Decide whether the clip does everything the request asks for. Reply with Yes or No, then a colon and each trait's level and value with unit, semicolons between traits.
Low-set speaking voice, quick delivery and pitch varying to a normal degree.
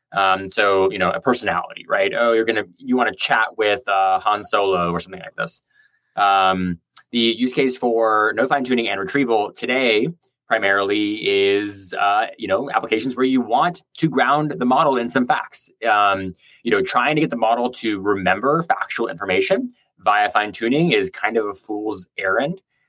No: low, 110 Hz; average, 185 wpm; average, 4.5 semitones